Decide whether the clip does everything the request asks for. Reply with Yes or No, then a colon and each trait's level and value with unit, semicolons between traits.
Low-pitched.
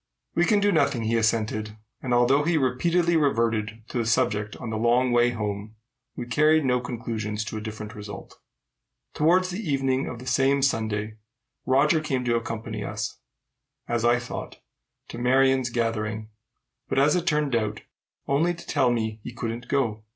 Yes: low, 120 Hz